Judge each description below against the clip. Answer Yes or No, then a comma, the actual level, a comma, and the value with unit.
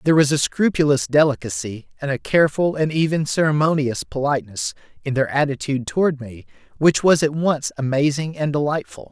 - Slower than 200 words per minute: Yes, average, 160 wpm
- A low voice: No, medium, 145 Hz